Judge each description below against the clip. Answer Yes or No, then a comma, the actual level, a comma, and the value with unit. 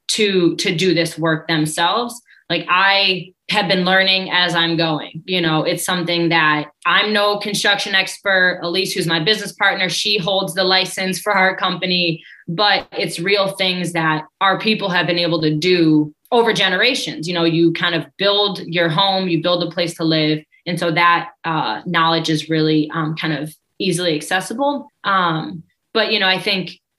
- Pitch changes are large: No, average, 2.8 semitones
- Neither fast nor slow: Yes, average, 180 wpm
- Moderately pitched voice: Yes, medium, 180 Hz